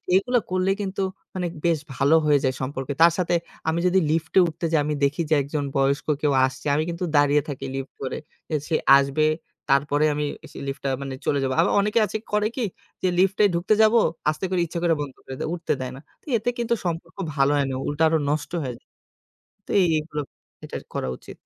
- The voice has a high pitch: No, medium, 155 Hz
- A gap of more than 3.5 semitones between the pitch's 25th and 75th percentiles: Yes, average, 4.3 semitones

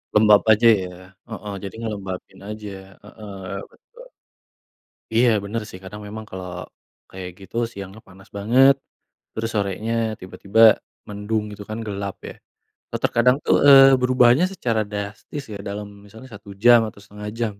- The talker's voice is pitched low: Yes, low, 105 Hz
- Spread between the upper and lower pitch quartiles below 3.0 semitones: Yes, narrow, 2.5 semitones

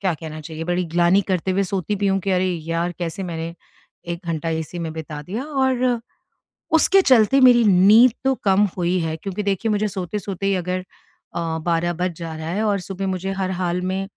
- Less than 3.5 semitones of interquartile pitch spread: Yes, average, 3.1 semitones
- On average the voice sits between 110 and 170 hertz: No, medium, 185 Hz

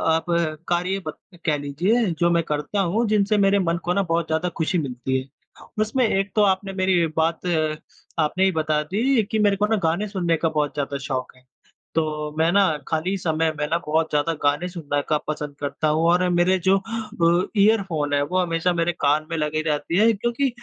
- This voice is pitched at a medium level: Yes, medium, 170 Hz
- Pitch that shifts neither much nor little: Yes, average, 4.2 semitones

